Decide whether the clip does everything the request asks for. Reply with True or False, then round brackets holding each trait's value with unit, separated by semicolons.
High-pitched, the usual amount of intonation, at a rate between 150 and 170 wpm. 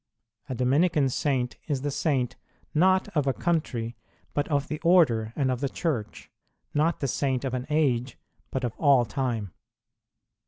False (135 Hz; 3.4 semitones; 160 wpm)